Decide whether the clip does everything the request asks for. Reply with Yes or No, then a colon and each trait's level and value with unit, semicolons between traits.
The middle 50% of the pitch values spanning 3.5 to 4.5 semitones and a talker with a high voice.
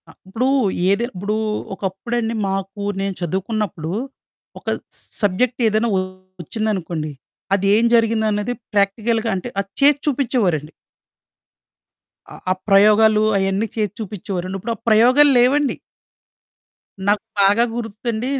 No: average, 3.0 semitones; high, 210 Hz